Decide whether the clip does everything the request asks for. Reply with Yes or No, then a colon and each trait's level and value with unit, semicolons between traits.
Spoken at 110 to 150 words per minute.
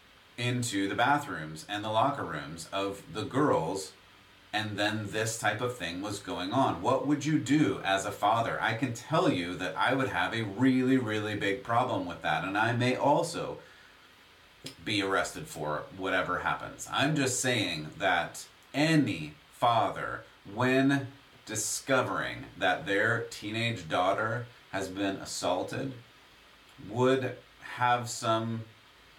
Yes: average, 140 wpm